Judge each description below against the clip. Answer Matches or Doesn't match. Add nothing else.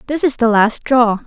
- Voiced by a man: Doesn't match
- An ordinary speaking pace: Doesn't match